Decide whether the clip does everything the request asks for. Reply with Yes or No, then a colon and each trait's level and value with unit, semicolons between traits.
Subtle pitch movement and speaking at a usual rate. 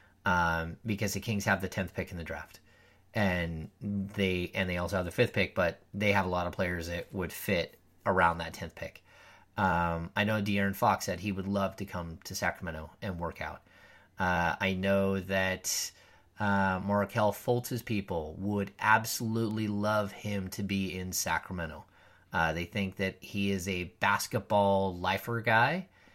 Yes: narrow, 2.3 semitones; average, 175 wpm